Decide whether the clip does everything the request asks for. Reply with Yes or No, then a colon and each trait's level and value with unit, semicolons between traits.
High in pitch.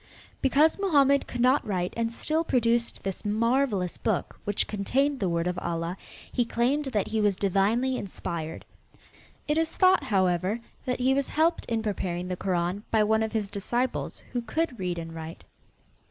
Yes: high, 220 Hz